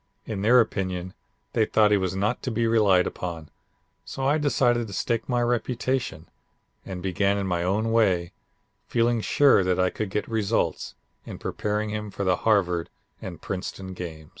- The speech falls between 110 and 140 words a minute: No, average, 170 wpm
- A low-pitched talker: Yes, low, 105 Hz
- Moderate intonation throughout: Yes, average, 3.9 semitones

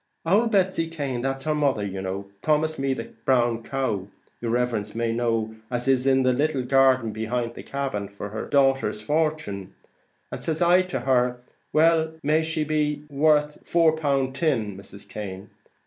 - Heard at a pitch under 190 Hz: Yes, low, 135 Hz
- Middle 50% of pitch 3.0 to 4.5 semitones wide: No, average, 5.2 semitones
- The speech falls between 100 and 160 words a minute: No, average, 180 wpm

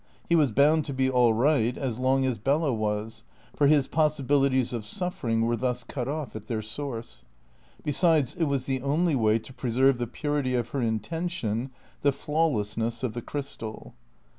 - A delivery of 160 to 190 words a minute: Yes, average, 175 wpm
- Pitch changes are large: No, average, 4.1 semitones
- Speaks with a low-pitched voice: Yes, low, 130 Hz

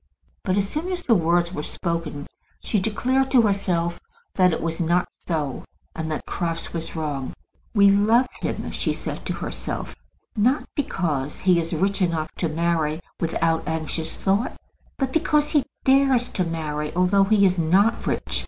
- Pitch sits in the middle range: Yes, medium, 175 Hz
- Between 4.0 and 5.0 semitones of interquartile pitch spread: Yes, average, 4.5 semitones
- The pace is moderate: Yes, average, 165 wpm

